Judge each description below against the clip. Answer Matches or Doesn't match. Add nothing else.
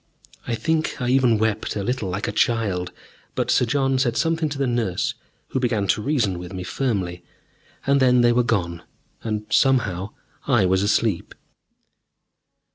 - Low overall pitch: Matches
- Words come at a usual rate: Matches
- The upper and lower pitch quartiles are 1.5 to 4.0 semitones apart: Doesn't match